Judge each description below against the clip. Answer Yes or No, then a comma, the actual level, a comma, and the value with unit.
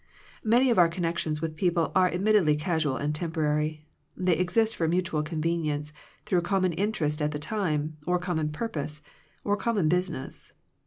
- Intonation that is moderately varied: Yes, average, 3.3 semitones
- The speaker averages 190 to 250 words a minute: No, average, 155 wpm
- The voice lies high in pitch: No, medium, 165 Hz